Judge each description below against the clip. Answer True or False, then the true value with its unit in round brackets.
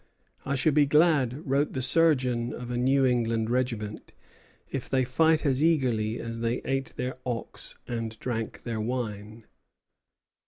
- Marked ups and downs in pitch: False (3.0 semitones)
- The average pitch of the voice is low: True (125 Hz)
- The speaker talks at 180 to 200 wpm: False (150 wpm)